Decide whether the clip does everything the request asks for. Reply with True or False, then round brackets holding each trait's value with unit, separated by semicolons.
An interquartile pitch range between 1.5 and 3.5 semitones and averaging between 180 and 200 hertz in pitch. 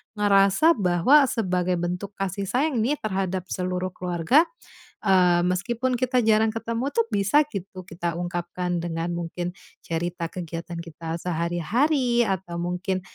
False (4.5 semitones; 185 Hz)